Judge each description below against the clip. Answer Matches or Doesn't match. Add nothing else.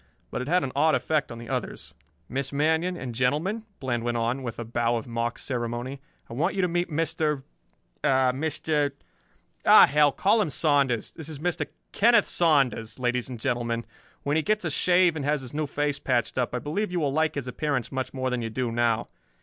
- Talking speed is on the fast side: Matches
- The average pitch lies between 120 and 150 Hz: Matches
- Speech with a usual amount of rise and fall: Matches